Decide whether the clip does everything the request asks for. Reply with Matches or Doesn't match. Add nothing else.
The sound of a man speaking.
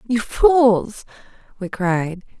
Doesn't match